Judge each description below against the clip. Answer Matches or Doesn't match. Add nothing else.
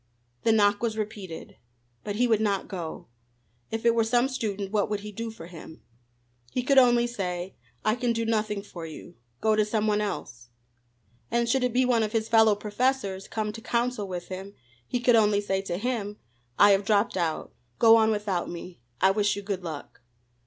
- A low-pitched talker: Doesn't match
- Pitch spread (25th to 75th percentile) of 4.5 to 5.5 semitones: Doesn't match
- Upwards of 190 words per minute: Matches